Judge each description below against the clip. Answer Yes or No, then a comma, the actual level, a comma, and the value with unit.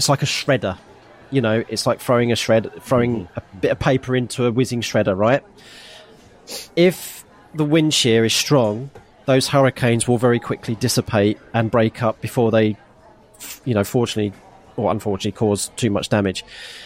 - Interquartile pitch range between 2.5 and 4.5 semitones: Yes, average, 3.1 semitones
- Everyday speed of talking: Yes, average, 165 wpm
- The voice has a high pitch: No, low, 120 Hz